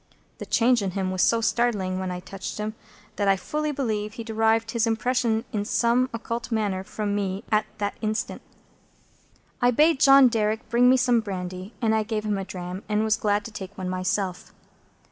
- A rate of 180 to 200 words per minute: Yes, average, 190 wpm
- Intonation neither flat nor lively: Yes, average, 3.1 semitones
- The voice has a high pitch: Yes, high, 215 Hz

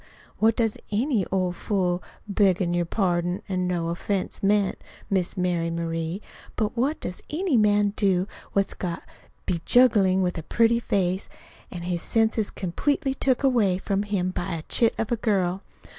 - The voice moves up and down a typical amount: Yes, average, 3.7 semitones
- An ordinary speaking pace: Yes, average, 160 wpm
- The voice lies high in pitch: Yes, high, 195 Hz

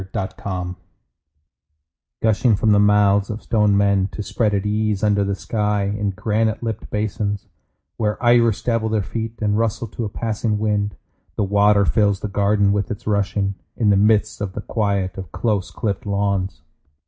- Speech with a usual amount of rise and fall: No, narrow, 1.4 semitones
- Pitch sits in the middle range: No, low, 105 Hz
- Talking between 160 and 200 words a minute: Yes, average, 175 wpm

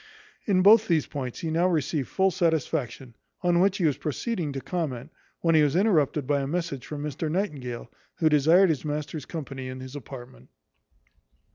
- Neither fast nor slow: Yes, average, 175 wpm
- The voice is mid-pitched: Yes, medium, 150 Hz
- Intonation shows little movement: No, average, 4.2 semitones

